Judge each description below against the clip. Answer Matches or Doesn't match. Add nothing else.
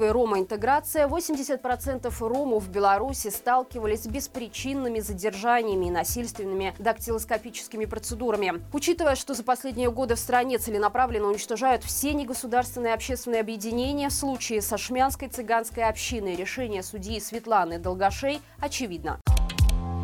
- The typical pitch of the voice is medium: Doesn't match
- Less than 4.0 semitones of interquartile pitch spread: Matches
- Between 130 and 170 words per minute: Doesn't match